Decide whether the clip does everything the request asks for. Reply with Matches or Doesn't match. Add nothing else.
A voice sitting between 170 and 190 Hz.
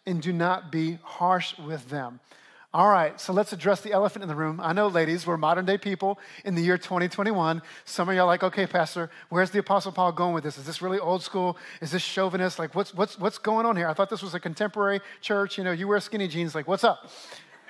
Matches